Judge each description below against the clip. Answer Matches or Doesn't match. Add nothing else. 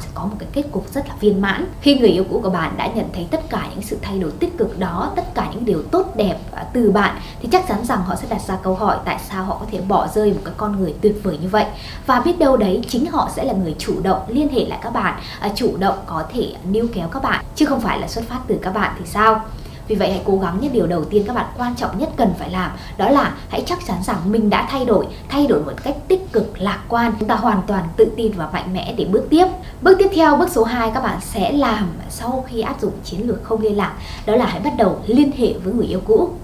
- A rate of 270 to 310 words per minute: Matches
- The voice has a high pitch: Matches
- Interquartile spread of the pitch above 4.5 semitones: Matches